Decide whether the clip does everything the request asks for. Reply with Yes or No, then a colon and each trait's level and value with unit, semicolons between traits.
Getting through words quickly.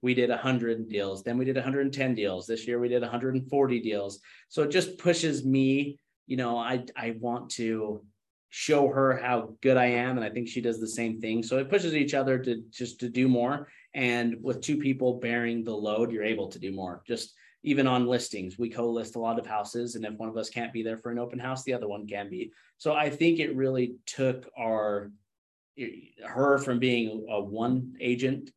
Yes: fast, 215 wpm